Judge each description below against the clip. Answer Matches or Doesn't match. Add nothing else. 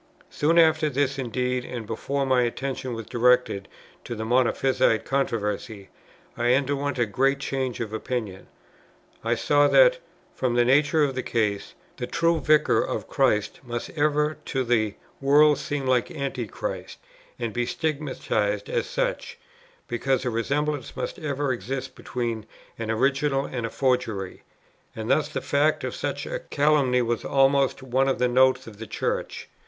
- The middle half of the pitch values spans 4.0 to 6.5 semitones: Doesn't match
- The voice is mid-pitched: Doesn't match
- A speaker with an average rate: Matches